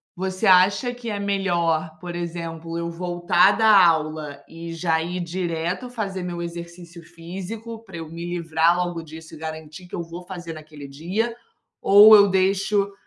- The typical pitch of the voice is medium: Yes, medium, 175 Hz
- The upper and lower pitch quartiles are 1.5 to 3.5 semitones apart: Yes, narrow, 2.6 semitones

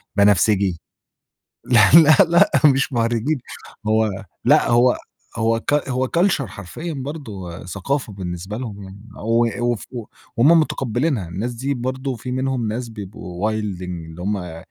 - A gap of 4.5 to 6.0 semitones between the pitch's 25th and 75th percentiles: Yes, average, 4.8 semitones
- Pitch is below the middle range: Yes, low, 115 Hz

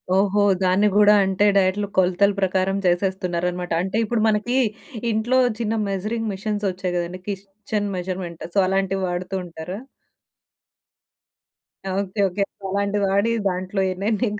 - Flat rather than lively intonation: Yes, narrow, 2.0 semitones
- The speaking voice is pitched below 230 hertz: Yes, high, 195 Hz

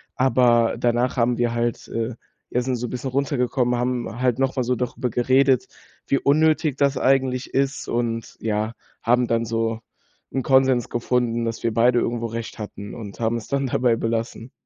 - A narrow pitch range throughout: Yes, narrow, 2.0 semitones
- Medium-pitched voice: No, low, 120 Hz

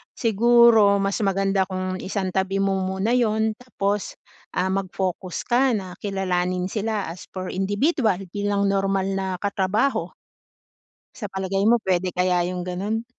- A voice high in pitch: Yes, high, 195 Hz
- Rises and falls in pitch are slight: Yes, narrow, 2.3 semitones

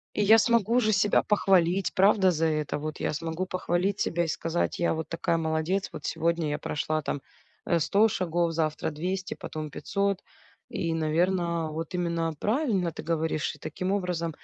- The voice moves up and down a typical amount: Yes, average, 3.1 semitones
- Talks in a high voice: No, medium, 170 Hz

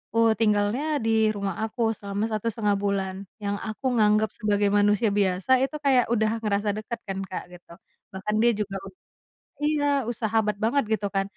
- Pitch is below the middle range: No, high, 210 Hz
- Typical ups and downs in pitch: No, narrow, 2.1 semitones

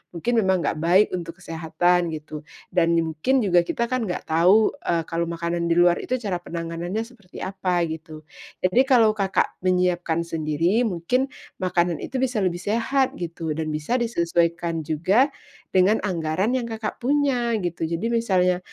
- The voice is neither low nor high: Yes, medium, 180 Hz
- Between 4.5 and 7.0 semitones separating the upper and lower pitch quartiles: Yes, average, 4.8 semitones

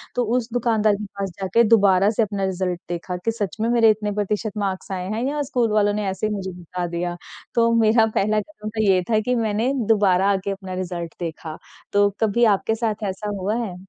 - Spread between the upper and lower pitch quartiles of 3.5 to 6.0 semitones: No, average, 2.7 semitones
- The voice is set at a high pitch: Yes, high, 205 Hz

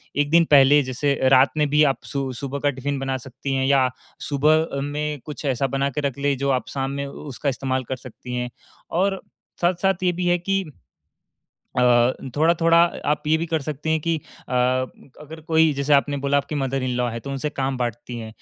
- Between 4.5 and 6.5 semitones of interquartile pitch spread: No, narrow, 2.4 semitones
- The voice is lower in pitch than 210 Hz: Yes, medium, 140 Hz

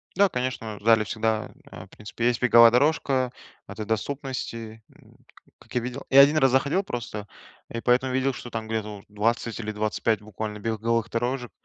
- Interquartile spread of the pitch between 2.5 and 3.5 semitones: Yes, average, 2.9 semitones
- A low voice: Yes, low, 115 Hz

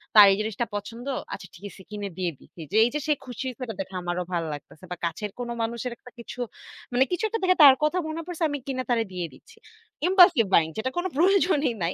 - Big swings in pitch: Yes, wide, 7.7 semitones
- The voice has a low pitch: No, high, 240 Hz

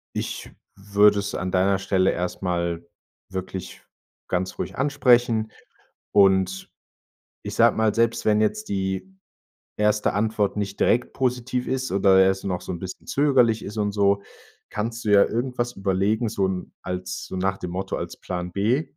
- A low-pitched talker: Yes, low, 100 Hz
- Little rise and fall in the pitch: No, average, 3.2 semitones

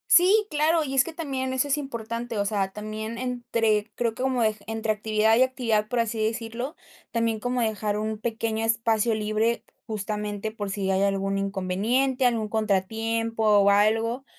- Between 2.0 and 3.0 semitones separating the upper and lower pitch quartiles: Yes, narrow, 2.5 semitones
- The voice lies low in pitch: No, high, 225 Hz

